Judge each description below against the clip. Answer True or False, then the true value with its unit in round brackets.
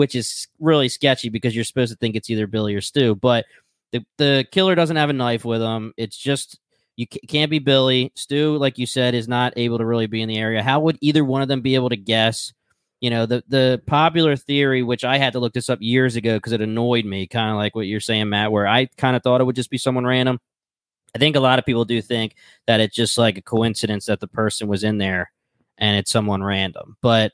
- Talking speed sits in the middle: False (255 wpm)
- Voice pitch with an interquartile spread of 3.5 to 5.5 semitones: False (3.0 semitones)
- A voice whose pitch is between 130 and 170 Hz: False (120 Hz)